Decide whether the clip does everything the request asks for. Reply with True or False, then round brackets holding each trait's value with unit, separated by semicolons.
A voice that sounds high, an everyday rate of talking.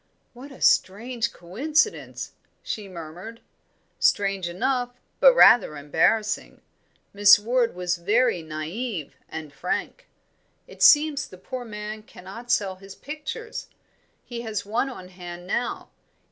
False (210 Hz; 120 wpm)